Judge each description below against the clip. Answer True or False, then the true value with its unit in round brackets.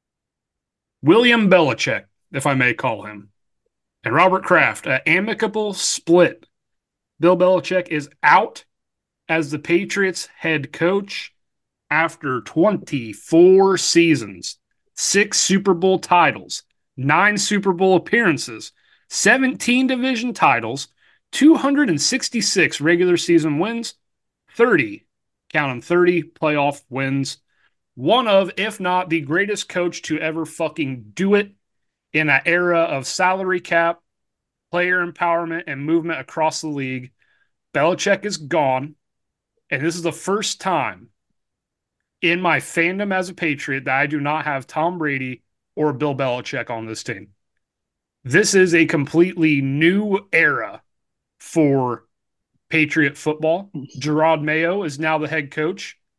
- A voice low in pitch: False (165 Hz)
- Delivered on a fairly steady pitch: False (4.6 semitones)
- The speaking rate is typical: False (125 wpm)